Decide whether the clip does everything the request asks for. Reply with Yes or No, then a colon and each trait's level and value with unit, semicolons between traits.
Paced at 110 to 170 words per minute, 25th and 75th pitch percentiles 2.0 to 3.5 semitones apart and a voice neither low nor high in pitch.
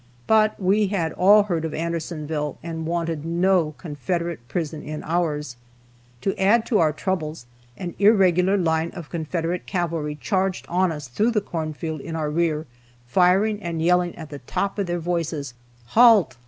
Yes: average, 165 wpm; average, 3.2 semitones; medium, 170 Hz